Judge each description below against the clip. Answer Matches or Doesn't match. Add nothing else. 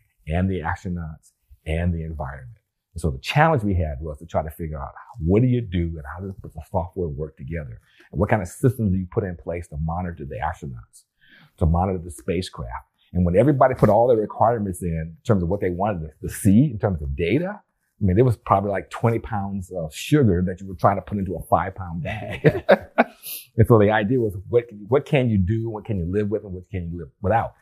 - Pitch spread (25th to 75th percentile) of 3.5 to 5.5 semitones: Matches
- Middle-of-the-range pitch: Doesn't match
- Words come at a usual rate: Doesn't match